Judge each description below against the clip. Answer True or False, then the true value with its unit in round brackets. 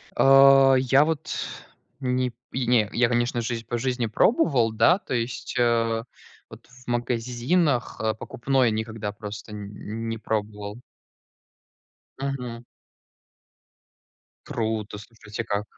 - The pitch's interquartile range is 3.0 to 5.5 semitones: False (2.6 semitones)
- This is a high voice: False (120 Hz)